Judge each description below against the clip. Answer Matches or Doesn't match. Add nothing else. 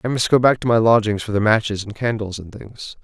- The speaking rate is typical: Doesn't match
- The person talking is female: Doesn't match